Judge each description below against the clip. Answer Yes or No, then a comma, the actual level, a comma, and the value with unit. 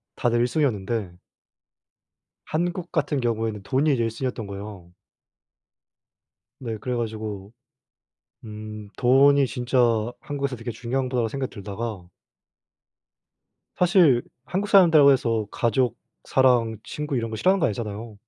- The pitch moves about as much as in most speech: Yes, average, 3.9 semitones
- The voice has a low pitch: Yes, low, 120 Hz